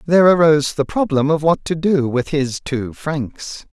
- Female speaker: No, male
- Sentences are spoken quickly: No, average, 190 wpm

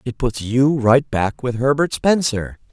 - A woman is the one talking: No, male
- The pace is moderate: Yes, average, 175 wpm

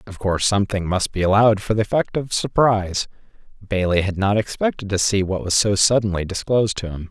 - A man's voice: Yes, male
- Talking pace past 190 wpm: Yes, fast, 205 wpm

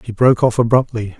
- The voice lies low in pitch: Yes, low, 115 Hz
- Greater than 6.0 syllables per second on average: Yes, 6.4 syllables/s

